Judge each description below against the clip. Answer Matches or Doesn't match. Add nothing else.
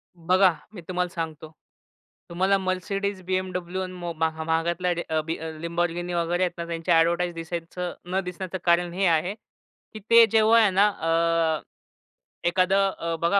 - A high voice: Doesn't match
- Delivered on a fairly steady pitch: Matches